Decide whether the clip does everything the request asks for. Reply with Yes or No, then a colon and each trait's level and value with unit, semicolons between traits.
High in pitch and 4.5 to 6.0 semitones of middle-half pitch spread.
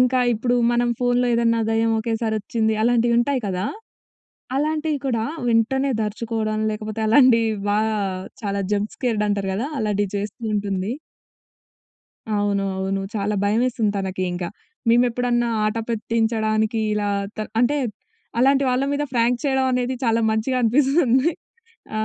No: high, 230 Hz; average, 2.8 semitones